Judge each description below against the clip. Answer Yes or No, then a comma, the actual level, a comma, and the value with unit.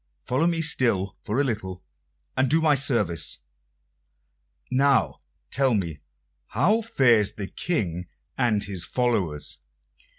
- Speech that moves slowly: Yes, slow, 120 wpm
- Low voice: Yes, low, 120 Hz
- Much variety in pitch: Yes, wide, 6.5 semitones